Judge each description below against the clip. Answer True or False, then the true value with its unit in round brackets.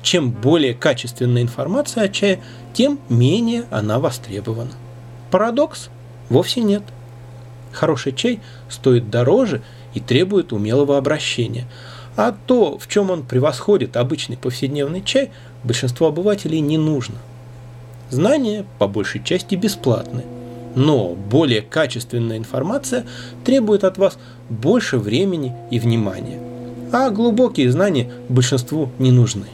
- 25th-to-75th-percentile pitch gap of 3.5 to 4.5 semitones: False (5.2 semitones)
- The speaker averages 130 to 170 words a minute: False (115 wpm)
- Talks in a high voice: False (125 Hz)